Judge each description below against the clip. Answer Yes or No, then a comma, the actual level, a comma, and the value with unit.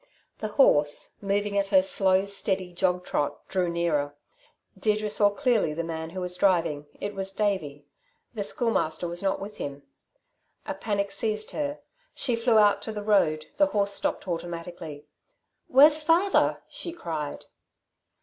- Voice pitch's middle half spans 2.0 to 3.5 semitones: No, average, 4.0 semitones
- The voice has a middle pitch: No, high, 195 Hz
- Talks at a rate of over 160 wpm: No, average, 150 wpm